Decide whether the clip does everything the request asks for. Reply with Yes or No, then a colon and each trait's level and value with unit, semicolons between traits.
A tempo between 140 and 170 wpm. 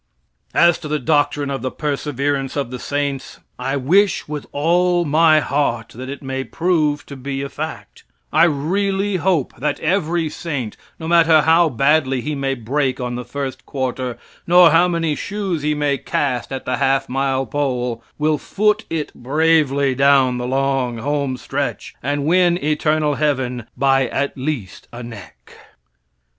Yes: average, 160 wpm